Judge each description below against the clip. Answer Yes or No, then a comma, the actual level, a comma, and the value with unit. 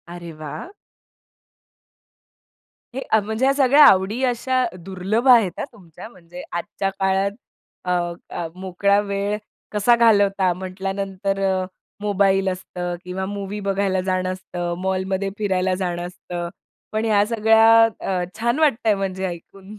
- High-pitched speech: Yes, high, 195 Hz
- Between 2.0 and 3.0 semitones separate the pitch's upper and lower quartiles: Yes, narrow, 2.6 semitones